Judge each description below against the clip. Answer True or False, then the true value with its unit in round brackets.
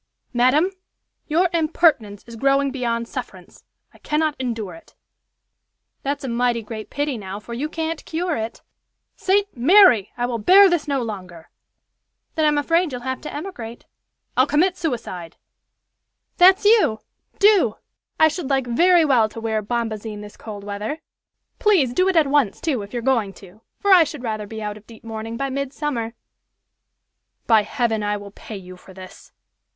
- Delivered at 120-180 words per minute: True (165 wpm)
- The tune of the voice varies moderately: False (6.2 semitones)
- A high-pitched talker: True (245 Hz)